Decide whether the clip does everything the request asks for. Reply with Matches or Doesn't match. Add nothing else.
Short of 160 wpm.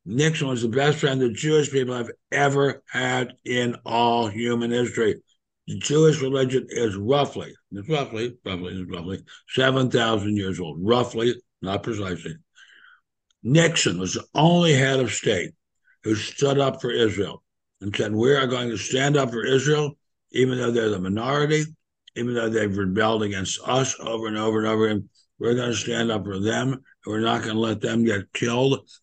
Doesn't match